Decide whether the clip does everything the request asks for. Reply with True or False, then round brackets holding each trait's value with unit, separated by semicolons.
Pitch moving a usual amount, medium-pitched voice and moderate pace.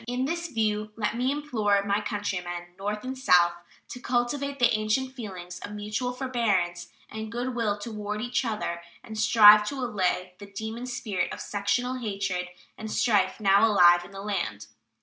False (3.6 semitones; 215 Hz; 170 wpm)